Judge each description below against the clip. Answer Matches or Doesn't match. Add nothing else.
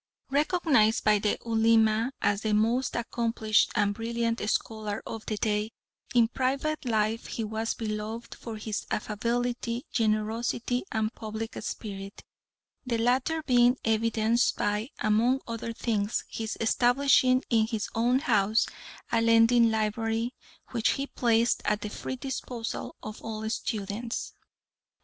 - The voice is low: Doesn't match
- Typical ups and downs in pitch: Doesn't match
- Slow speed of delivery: Matches